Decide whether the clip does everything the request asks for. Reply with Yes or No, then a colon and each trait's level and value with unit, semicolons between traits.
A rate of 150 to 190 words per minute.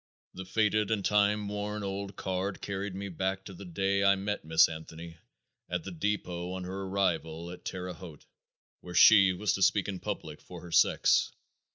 Yes: average, 185 wpm